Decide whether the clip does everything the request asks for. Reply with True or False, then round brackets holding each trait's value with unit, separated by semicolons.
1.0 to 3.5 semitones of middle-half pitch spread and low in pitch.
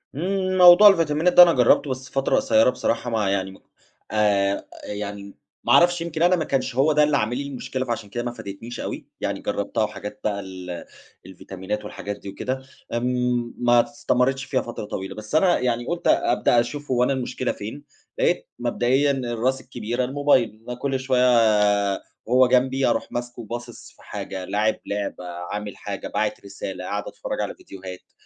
False (4.5 semitones; 120 Hz)